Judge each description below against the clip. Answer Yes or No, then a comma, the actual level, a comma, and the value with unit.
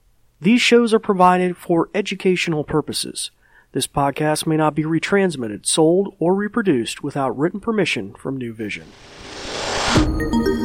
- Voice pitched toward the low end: No, medium, 155 Hz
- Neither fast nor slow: No, slow, 125 wpm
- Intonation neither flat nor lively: No, wide, 7.4 semitones